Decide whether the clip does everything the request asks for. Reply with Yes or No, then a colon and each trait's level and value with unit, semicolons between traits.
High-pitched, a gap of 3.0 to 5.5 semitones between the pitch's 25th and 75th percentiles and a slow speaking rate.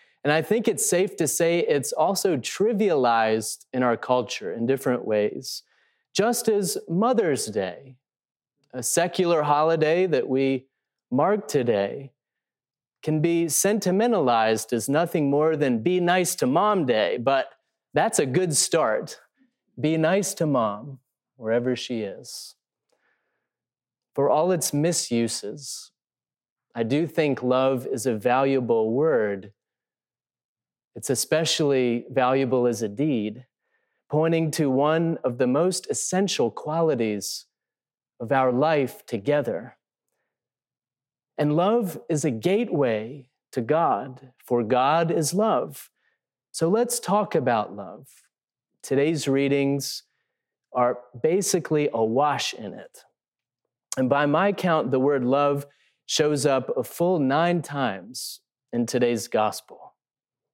No: medium, 145 Hz; average, 5.1 semitones; slow, 120 wpm